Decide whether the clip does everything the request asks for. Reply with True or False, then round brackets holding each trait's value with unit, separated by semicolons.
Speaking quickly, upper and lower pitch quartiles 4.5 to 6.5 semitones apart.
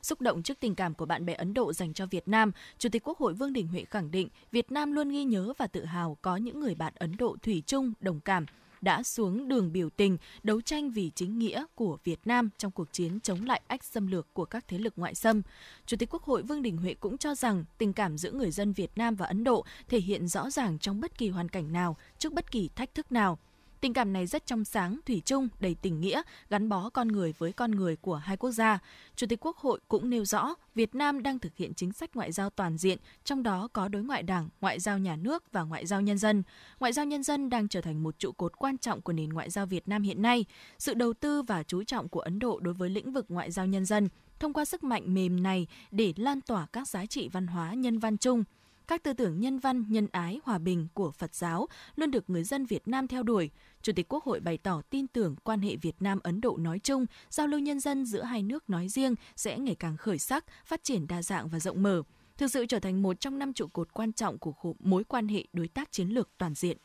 True (260 wpm; 5.3 semitones)